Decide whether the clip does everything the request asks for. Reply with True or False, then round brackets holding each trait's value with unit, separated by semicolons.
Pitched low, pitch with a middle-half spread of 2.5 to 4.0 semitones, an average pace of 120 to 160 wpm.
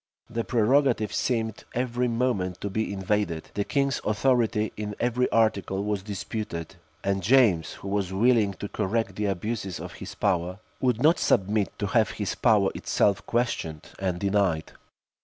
True (105 Hz; 3.4 semitones; 155 wpm)